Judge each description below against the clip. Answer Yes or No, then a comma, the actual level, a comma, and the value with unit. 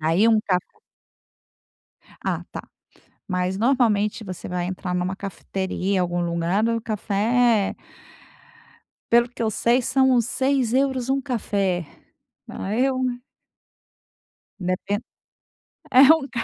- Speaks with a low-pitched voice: No, high, 210 Hz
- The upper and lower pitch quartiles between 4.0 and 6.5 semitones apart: Yes, average, 4.9 semitones